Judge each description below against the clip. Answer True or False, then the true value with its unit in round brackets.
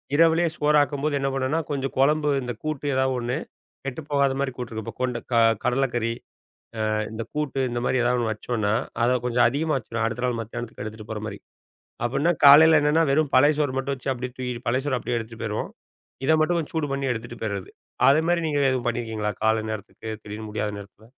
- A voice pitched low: True (130 Hz)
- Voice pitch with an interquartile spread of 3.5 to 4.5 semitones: True (4.0 semitones)